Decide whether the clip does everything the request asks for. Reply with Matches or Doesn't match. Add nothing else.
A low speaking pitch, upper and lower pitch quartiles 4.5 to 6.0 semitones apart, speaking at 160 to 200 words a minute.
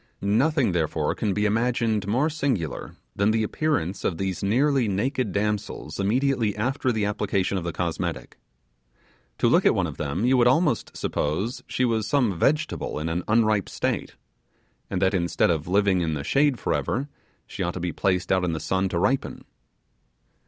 Matches